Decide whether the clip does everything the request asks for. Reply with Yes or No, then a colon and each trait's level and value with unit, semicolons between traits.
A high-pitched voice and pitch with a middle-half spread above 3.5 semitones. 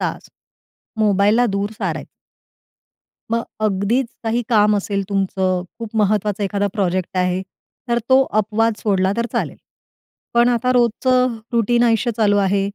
No: high, 210 Hz; average, 2.9 semitones